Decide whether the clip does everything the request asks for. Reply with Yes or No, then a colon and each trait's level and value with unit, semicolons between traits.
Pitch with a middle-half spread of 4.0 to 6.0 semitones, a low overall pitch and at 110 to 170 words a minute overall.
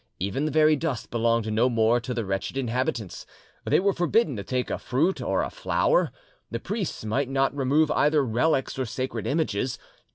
No: average, 4.8 semitones; low, 130 Hz; average, 185 wpm